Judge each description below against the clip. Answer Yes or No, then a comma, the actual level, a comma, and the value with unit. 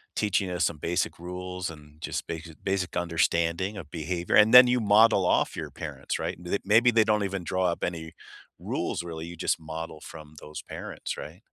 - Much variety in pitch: No, average, 3.2 semitones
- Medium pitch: No, very low, 90 Hz